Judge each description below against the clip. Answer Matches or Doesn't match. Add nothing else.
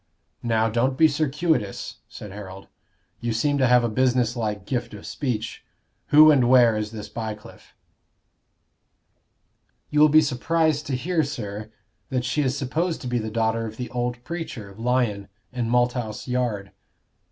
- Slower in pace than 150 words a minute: Doesn't match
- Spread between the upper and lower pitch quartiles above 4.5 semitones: Doesn't match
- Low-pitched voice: Matches